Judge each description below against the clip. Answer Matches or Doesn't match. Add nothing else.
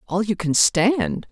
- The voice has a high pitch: Matches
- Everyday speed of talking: Matches